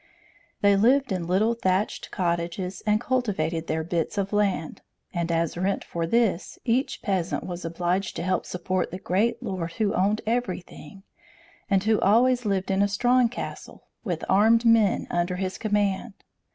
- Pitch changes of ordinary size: Yes, average, 3.7 semitones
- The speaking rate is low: No, average, 160 wpm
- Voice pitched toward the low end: No, high, 195 Hz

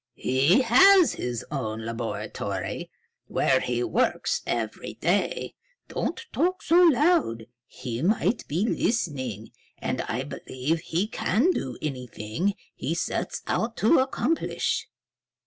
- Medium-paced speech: No, slow, 115 wpm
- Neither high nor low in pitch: Yes, medium, 170 Hz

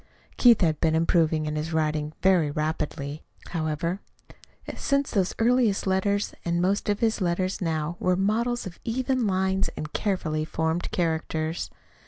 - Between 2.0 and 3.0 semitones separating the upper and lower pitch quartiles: No, average, 4.3 semitones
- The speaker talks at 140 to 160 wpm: Yes, average, 145 wpm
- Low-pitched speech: No, medium, 175 Hz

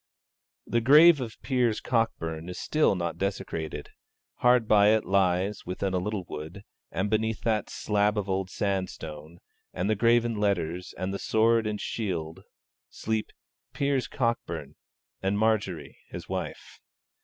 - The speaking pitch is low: Yes, low, 105 Hz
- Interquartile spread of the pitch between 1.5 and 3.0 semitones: No, average, 3.7 semitones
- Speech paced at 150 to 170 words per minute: No, average, 140 wpm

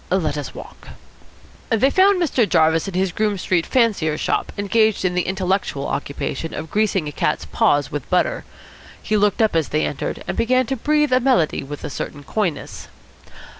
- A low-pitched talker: No, high, 190 Hz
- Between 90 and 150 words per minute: No, average, 180 wpm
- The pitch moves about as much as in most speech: No, wide, 6.4 semitones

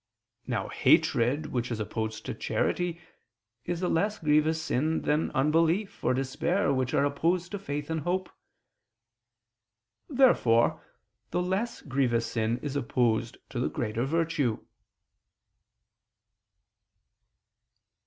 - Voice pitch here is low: No, medium, 145 Hz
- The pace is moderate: No, slow, 115 wpm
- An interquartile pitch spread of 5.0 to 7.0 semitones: Yes, wide, 5.6 semitones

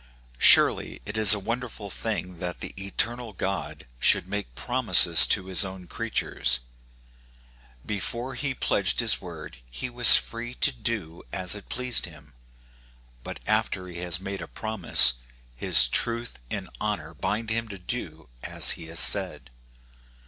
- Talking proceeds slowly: No, average, 150 wpm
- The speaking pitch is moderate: No, low, 100 Hz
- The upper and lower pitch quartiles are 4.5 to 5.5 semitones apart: Yes, average, 5.1 semitones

